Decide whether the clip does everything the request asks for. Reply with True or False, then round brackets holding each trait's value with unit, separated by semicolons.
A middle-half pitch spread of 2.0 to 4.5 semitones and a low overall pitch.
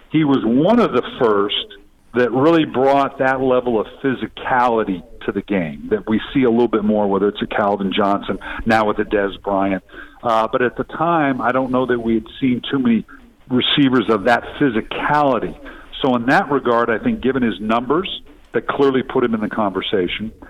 True (3.9 semitones; 120 Hz)